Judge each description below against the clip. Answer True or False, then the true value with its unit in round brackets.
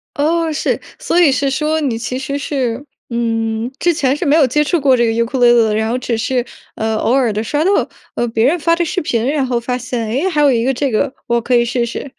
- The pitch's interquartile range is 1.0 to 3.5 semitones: False (4.0 semitones)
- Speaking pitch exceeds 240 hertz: True (255 Hz)